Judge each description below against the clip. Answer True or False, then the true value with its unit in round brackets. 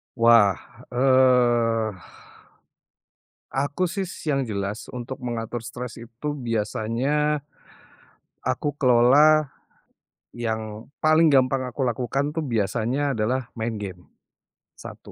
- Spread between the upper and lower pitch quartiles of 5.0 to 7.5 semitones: False (3.7 semitones)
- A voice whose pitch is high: False (125 Hz)